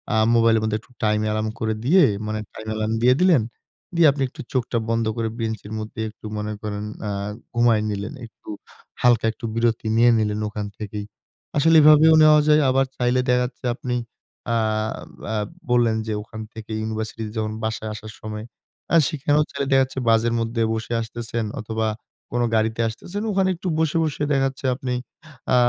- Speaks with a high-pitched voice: No, low, 115 Hz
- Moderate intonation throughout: Yes, average, 3.5 semitones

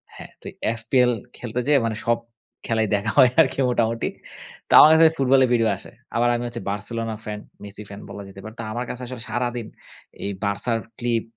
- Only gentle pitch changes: Yes, narrow, 2.1 semitones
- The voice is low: Yes, low, 115 Hz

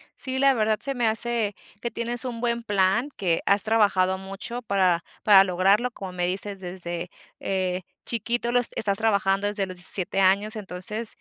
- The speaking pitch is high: Yes, high, 205 Hz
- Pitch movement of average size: Yes, average, 3.7 semitones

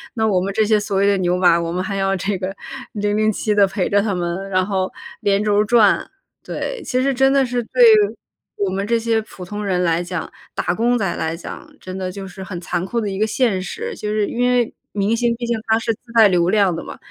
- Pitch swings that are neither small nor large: Yes, average, 3.1 semitones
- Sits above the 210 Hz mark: No, high, 200 Hz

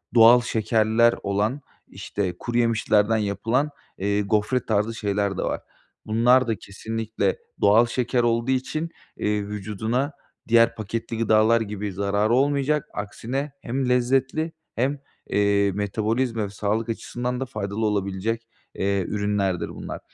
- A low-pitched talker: Yes, low, 110 Hz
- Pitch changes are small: No, average, 3.0 semitones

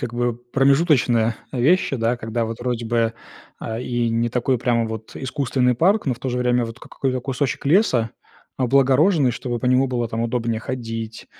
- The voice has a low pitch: Yes, low, 125 Hz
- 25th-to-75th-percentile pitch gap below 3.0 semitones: Yes, narrow, 2.4 semitones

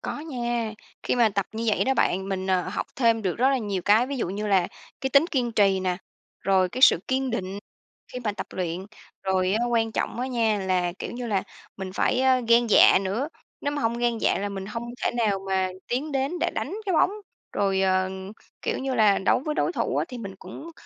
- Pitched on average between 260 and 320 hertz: No, high, 220 Hz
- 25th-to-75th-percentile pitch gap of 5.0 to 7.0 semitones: No, average, 4.6 semitones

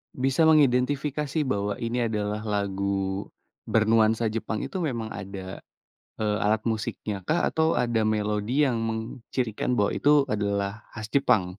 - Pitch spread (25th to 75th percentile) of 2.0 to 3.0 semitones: No, average, 3.8 semitones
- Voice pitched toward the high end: No, low, 110 Hz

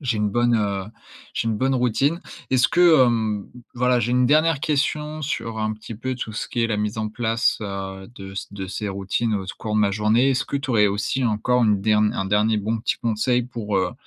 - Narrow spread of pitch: No, average, 3.2 semitones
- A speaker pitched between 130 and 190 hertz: No, low, 110 Hz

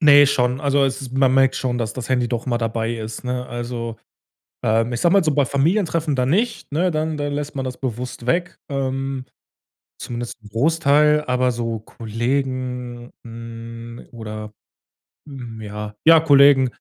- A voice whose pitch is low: Yes, low, 130 Hz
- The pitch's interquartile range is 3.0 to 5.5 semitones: Yes, average, 3.4 semitones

